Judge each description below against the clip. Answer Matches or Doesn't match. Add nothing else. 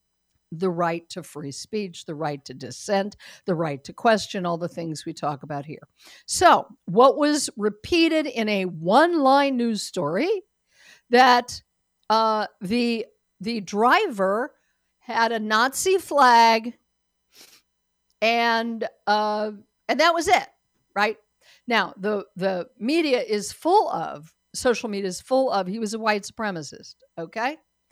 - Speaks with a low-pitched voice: Doesn't match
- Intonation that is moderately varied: Doesn't match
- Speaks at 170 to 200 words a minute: Doesn't match